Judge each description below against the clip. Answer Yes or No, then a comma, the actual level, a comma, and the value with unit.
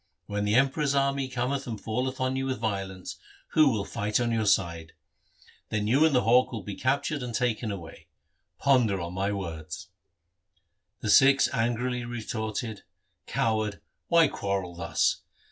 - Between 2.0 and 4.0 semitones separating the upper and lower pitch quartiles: No, average, 4.5 semitones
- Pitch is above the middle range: No, low, 115 Hz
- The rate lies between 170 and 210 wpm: No, average, 160 wpm